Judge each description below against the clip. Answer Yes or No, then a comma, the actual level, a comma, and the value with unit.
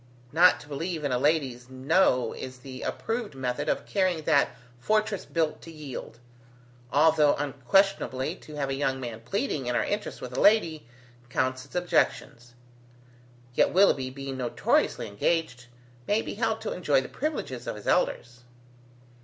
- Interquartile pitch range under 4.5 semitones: No, average, 5.2 semitones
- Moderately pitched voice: Yes, medium, 145 Hz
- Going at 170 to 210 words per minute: No, average, 155 wpm